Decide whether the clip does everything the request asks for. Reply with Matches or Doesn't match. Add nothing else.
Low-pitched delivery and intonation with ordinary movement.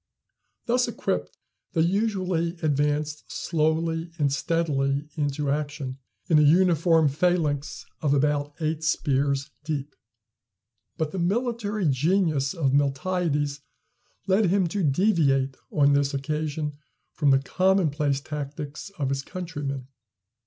Doesn't match